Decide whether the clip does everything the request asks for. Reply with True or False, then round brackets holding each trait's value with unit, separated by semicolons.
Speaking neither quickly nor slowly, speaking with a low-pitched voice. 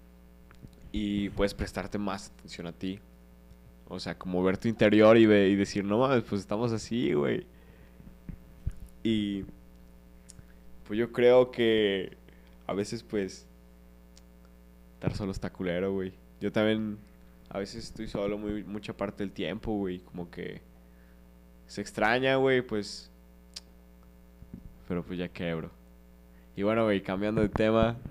True (135 wpm; 95 Hz)